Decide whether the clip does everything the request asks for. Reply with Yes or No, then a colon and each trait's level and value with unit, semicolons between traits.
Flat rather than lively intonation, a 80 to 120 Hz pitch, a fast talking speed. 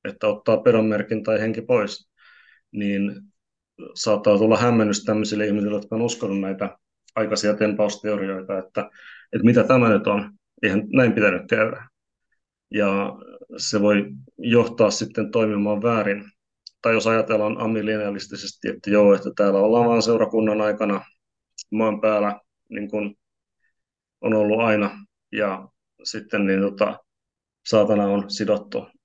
No: narrow, 1.4 semitones; low, 105 Hz; average, 125 wpm